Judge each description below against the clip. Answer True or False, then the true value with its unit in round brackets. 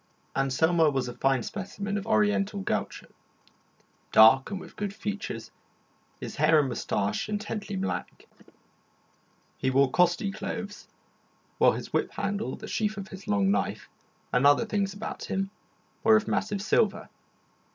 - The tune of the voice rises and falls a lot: True (7.2 semitones)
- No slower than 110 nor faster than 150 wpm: True (145 wpm)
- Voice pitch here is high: True (195 Hz)